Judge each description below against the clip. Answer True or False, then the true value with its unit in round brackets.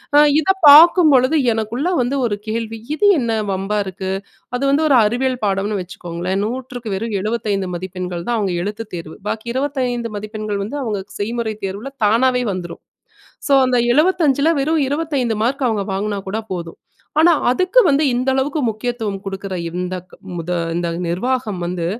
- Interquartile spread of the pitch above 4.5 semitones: True (5.2 semitones)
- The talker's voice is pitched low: False (225 Hz)